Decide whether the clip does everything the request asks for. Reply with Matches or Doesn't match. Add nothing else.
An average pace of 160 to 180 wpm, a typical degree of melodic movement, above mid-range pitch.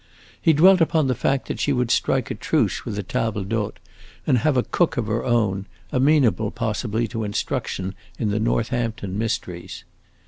Doesn't match